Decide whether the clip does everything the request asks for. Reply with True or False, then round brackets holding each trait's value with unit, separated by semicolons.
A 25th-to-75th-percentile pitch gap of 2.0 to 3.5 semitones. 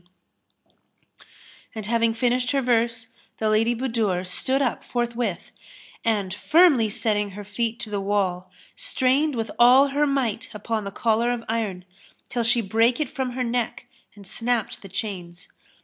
True (3.0 semitones)